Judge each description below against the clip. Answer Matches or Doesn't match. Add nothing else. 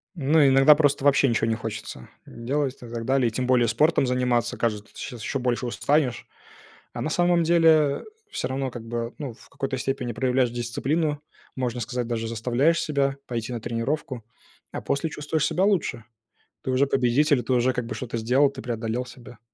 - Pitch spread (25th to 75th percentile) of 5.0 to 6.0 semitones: Doesn't match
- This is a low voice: Matches